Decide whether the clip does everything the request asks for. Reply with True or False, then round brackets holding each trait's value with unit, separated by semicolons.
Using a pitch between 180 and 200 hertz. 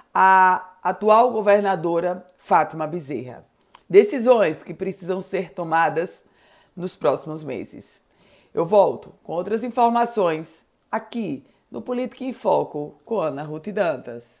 True (185 Hz)